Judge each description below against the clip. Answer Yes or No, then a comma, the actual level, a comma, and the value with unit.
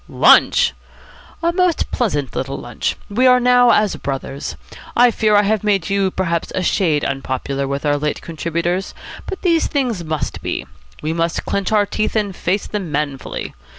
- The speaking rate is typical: Yes, average, 170 wpm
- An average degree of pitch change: No, wide, 6.4 semitones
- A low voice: No, medium, 185 Hz